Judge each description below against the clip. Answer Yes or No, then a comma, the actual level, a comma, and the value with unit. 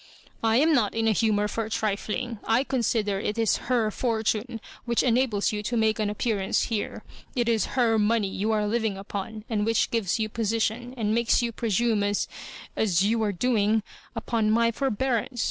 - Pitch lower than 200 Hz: No, high, 225 Hz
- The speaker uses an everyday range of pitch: No, narrow, 2.0 semitones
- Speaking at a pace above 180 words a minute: Yes, average, 190 wpm